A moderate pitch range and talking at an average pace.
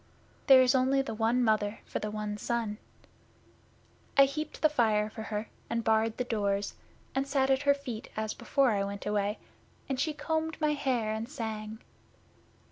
Yes: average, 4.2 semitones; average, 175 wpm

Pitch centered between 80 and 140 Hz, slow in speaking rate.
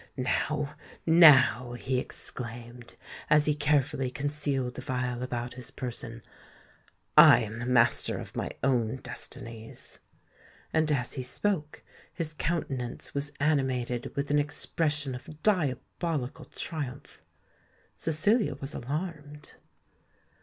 Yes: low, 135 Hz; slow, 110 wpm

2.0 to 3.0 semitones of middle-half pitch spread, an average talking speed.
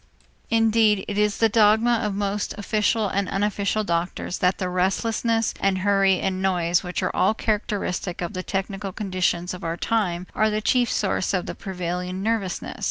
Yes: average, 2.7 semitones; average, 170 wpm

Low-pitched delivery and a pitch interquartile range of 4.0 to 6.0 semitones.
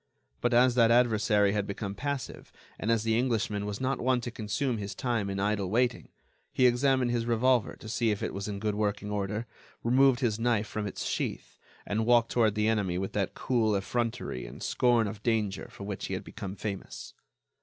No: low, 110 Hz; average, 2.9 semitones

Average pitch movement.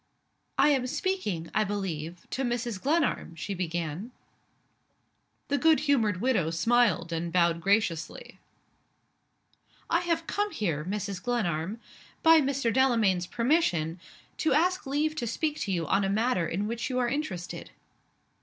No: wide, 7.9 semitones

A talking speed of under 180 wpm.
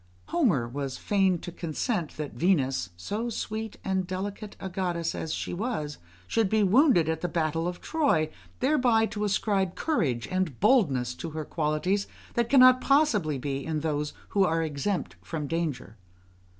Yes: average, 160 wpm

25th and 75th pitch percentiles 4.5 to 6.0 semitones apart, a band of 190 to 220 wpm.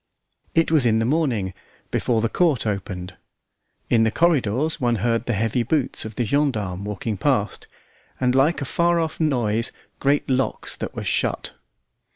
No: average, 5.1 semitones; average, 165 wpm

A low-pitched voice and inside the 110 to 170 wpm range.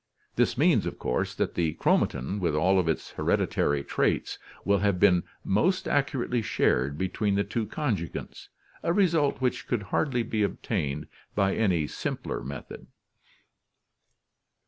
Yes: low, 100 Hz; average, 145 wpm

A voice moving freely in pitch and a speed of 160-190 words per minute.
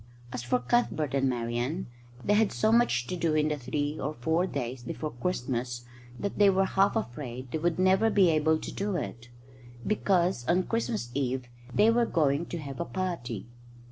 Yes: wide, 7.1 semitones; average, 185 wpm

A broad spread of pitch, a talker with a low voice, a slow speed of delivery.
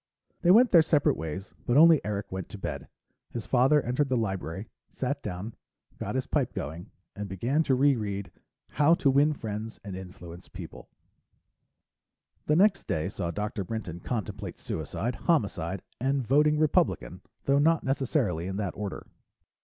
No: wide, 6.9 semitones; low, 115 Hz; average, 155 wpm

